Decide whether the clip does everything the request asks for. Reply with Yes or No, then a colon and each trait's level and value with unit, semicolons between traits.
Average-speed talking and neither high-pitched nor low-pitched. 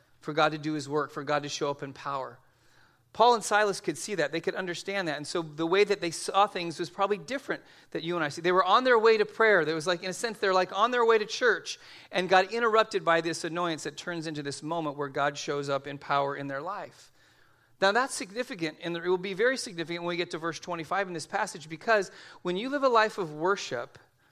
No: fast, 260 wpm; medium, 175 Hz